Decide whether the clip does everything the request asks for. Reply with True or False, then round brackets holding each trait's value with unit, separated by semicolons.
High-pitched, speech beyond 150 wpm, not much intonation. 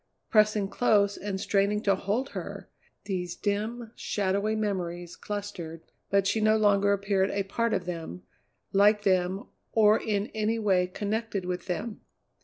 False (200 Hz; 145 wpm; 2.2 semitones)